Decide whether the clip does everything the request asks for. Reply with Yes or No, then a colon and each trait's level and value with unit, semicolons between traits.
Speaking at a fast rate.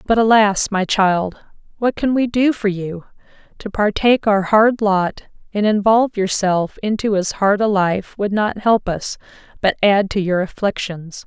No: average, 165 wpm